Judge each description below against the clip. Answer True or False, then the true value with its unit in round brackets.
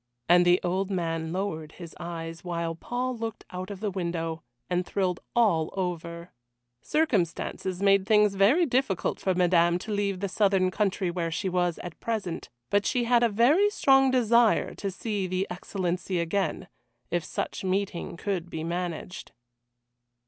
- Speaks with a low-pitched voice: False (185 Hz)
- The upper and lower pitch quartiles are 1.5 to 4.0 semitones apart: True (3.2 semitones)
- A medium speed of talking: True (155 wpm)